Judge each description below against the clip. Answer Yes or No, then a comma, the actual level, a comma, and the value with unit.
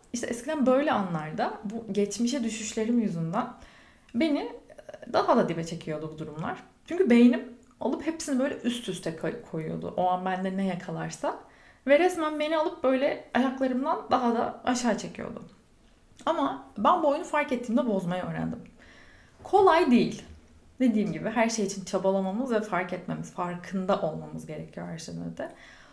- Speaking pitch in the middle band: No, high, 225 Hz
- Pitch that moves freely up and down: Yes, wide, 6.3 semitones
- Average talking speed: No, fast, 145 wpm